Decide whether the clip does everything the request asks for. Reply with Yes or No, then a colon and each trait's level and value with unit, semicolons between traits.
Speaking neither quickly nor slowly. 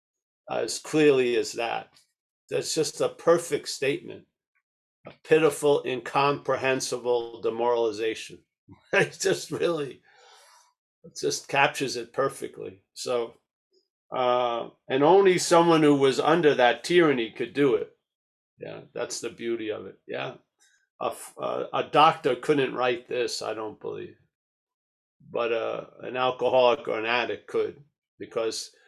No: slow, 125 wpm